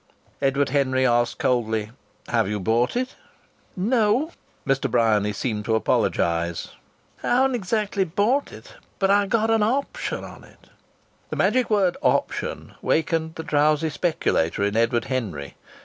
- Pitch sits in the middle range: Yes, medium, 145 Hz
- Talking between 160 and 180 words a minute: No, average, 140 wpm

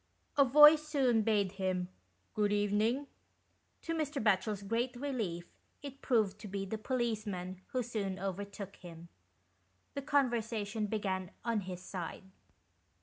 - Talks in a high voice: Yes, high, 210 Hz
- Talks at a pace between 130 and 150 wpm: Yes, average, 140 wpm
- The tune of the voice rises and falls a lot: No, average, 4.5 semitones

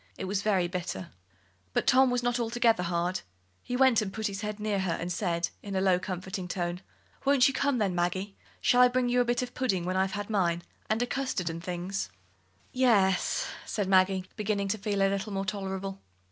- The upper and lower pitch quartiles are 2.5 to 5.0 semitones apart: Yes, average, 4.1 semitones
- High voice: Yes, high, 195 Hz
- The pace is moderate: No, fast, 220 wpm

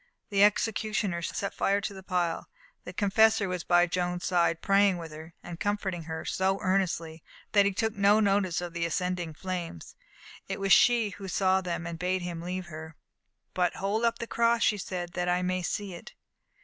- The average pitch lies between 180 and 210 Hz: Yes, medium, 185 Hz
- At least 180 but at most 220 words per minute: Yes, average, 190 wpm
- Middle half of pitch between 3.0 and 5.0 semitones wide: No, narrow, 2.5 semitones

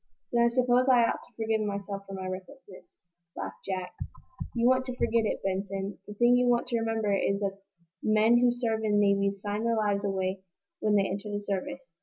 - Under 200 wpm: No, fast, 205 wpm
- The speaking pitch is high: Yes, high, 210 Hz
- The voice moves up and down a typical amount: Yes, average, 3.2 semitones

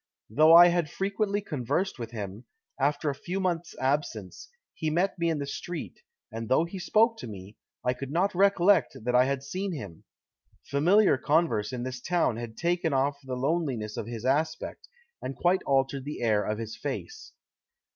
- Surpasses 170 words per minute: Yes, average, 180 wpm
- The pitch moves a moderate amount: No, wide, 6.0 semitones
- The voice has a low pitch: No, medium, 145 Hz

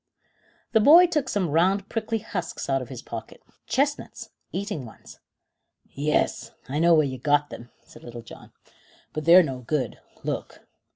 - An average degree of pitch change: No, wide, 7.5 semitones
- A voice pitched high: No, medium, 155 Hz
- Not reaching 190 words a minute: Yes, average, 160 wpm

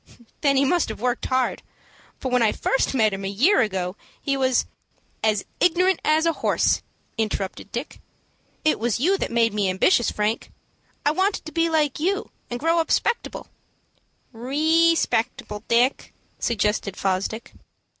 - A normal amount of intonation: No, wide, 6.7 semitones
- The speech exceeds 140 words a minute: Yes, average, 160 wpm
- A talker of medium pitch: No, very high, 255 Hz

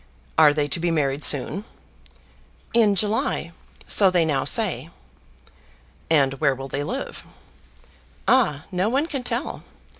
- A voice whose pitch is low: No, medium, 170 Hz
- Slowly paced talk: Yes, slow, 130 wpm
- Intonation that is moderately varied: No, wide, 7.1 semitones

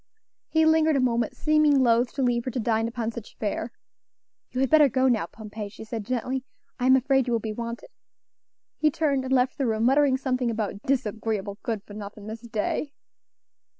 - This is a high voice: Yes, high, 240 Hz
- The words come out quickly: No, average, 195 wpm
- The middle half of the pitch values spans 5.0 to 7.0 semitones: No, average, 3.3 semitones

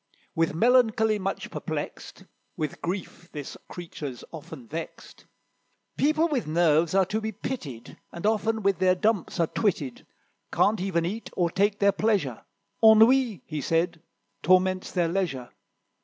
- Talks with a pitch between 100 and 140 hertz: No, medium, 185 Hz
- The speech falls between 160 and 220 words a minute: No, average, 140 wpm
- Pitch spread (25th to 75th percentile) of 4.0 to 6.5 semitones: Yes, average, 4.9 semitones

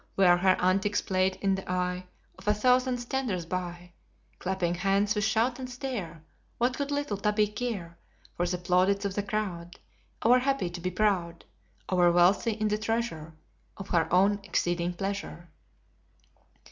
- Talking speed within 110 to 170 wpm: Yes, average, 160 wpm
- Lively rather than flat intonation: No, average, 3.4 semitones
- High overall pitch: Yes, high, 195 Hz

